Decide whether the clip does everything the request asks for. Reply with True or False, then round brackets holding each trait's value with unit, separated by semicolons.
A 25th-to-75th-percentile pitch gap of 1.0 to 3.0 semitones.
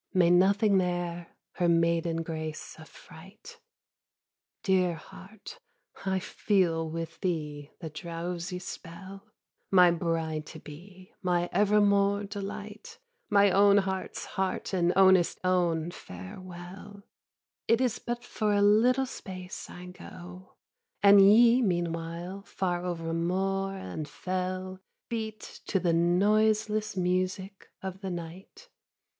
True (2.7 semitones)